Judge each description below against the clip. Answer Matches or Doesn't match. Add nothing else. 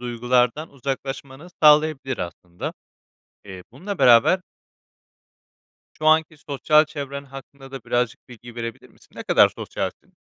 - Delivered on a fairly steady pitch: Doesn't match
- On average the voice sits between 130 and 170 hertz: Matches